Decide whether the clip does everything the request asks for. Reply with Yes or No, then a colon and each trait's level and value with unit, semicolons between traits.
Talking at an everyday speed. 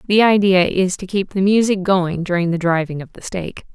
No: fast, 225 wpm